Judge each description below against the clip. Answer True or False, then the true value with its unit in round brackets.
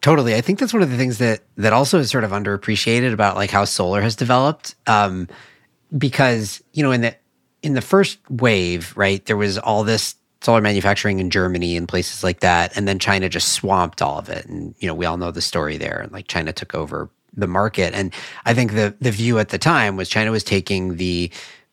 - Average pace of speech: False (225 wpm)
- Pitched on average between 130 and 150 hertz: False (105 Hz)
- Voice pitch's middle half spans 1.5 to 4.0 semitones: False (4.4 semitones)